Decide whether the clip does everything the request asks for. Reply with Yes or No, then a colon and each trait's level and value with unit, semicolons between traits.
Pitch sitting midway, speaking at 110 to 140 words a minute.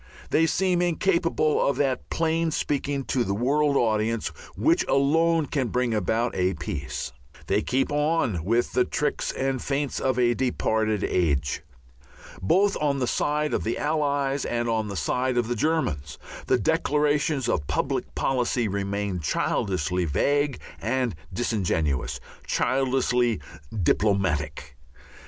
No: low, 125 Hz; slow, 135 wpm